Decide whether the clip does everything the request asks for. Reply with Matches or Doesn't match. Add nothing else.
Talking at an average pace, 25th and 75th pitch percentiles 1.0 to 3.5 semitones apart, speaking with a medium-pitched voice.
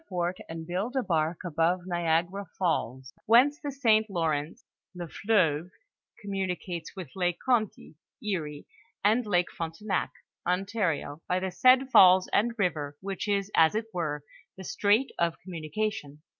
Doesn't match